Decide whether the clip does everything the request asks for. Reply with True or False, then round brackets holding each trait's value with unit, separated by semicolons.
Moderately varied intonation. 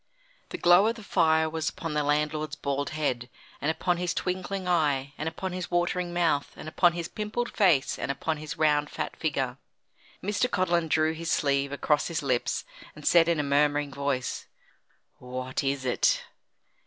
True (3.6 semitones)